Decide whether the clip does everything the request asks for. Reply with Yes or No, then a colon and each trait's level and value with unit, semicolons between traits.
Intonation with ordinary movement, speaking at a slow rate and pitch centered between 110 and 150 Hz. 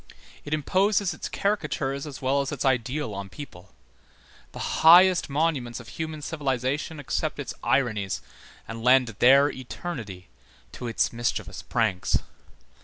Yes: average, 4.5 semitones; slow, 130 wpm; low, 135 Hz